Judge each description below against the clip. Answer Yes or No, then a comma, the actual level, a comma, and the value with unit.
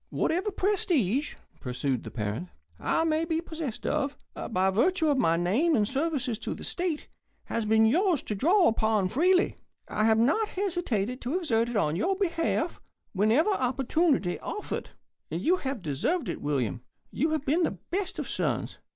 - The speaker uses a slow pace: No, average, 165 wpm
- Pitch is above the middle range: Yes, very high, 275 Hz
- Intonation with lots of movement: Yes, wide, 8.2 semitones